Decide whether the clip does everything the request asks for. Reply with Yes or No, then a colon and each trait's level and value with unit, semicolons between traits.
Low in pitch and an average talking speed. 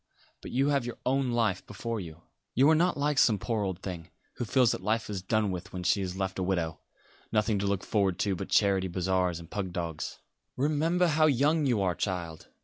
No: low, 100 Hz; fast, 220 wpm